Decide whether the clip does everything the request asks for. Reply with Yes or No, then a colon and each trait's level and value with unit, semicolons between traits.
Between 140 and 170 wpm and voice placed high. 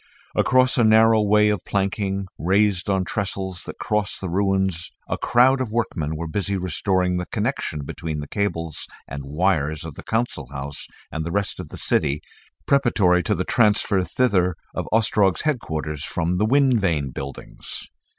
No: average, 165 wpm; very low, 95 Hz